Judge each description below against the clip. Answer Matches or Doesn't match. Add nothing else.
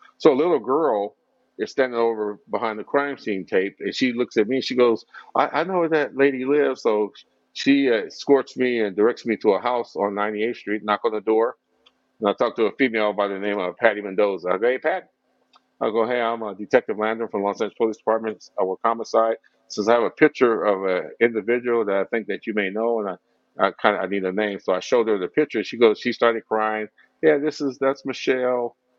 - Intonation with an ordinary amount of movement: Matches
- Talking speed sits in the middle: Doesn't match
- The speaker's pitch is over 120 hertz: Doesn't match